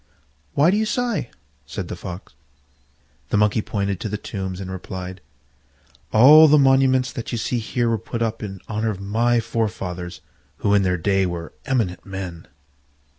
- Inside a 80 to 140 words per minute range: No, average, 170 wpm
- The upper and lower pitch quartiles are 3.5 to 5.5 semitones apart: Yes, average, 4.3 semitones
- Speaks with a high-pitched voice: No, low, 105 Hz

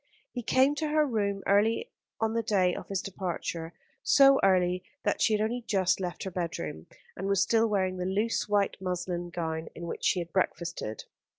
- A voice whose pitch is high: Yes, high, 195 Hz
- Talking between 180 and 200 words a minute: Yes, average, 190 wpm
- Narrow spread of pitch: No, average, 3.9 semitones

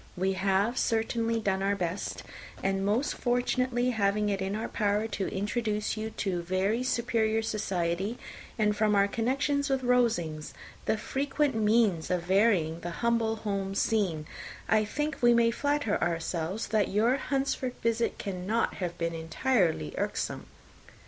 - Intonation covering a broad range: No, average, 3.6 semitones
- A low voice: No, high, 210 Hz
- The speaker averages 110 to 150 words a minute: Yes, average, 145 wpm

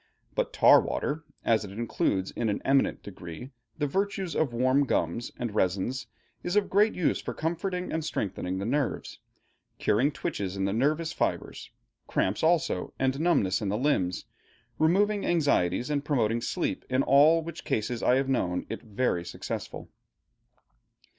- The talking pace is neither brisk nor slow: Yes, average, 155 wpm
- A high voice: No, low, 130 Hz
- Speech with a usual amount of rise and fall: No, wide, 7.5 semitones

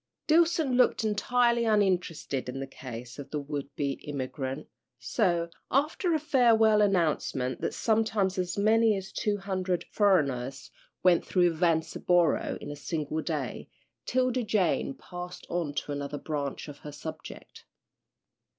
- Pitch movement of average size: No, wide, 6.9 semitones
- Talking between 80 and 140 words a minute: Yes, slow, 135 wpm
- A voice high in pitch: No, medium, 175 Hz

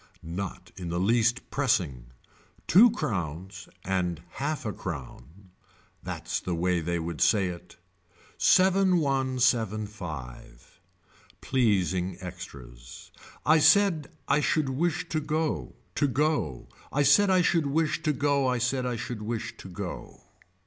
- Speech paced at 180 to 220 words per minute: No, average, 140 wpm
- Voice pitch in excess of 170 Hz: No, low, 115 Hz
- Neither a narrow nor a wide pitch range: No, wide, 8.6 semitones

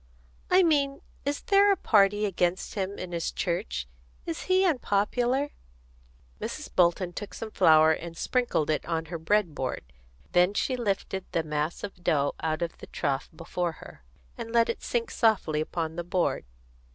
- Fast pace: No, average, 165 wpm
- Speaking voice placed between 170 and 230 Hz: Yes, medium, 185 Hz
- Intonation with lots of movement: Yes, wide, 5.9 semitones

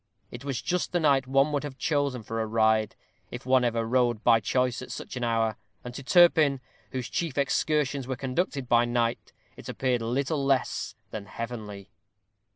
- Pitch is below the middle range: Yes, low, 125 Hz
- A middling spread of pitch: Yes, average, 3.2 semitones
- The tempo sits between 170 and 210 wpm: Yes, average, 180 wpm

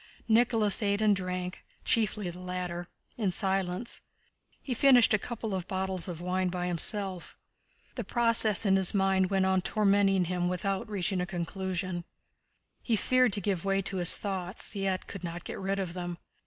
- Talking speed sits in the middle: Yes, average, 170 wpm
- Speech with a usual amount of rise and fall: No, narrow, 2.1 semitones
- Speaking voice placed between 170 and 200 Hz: Yes, high, 190 Hz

